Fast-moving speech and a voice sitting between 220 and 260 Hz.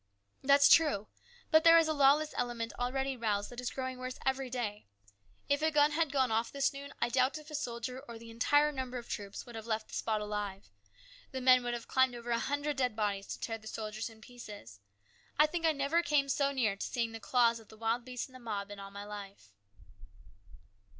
Yes: fast, 225 wpm; high, 245 Hz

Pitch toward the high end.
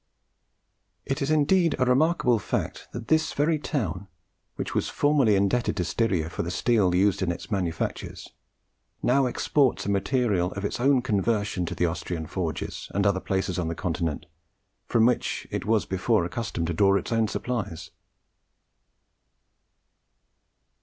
No: low, 100 Hz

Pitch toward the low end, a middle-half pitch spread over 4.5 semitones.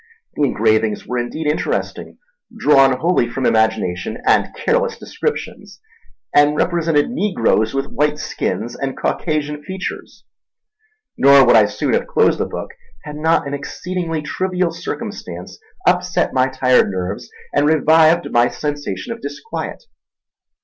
No: medium, 145 Hz; average, 5.1 semitones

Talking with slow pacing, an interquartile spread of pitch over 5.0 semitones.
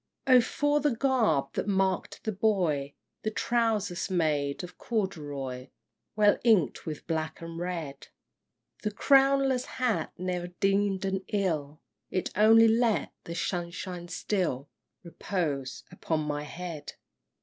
Yes: slow, 125 wpm; wide, 5.6 semitones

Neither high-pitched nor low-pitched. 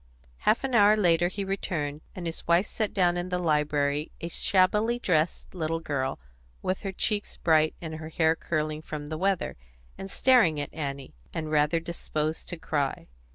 Yes: medium, 165 Hz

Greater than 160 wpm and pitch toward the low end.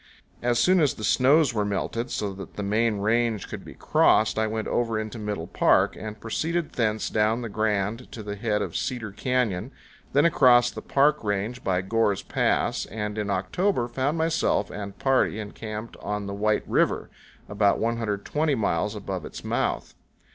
Yes: average, 175 wpm; low, 110 Hz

